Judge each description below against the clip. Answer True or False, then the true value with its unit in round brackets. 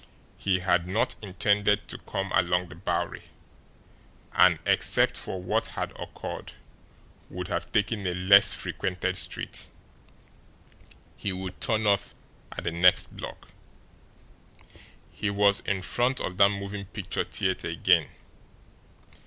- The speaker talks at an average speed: False (125 wpm)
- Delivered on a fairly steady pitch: True (2.0 semitones)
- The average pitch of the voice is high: False (95 Hz)